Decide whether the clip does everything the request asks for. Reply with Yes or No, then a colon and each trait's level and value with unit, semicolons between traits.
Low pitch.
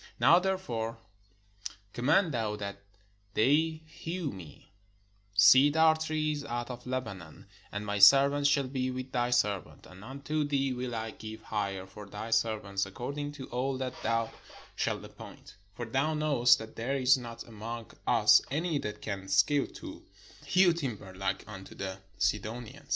Yes: low, 120 Hz